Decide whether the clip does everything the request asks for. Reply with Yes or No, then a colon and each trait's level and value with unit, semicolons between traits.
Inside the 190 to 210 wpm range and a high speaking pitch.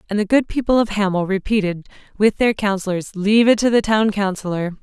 Yes: average, 200 wpm; high, 205 Hz